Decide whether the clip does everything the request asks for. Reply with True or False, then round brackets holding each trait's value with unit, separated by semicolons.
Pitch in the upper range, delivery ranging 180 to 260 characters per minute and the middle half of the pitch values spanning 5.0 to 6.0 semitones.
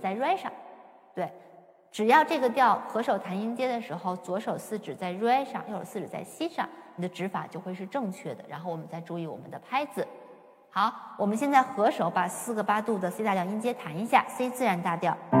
False (205 Hz; 310 characters per minute; 5.5 semitones)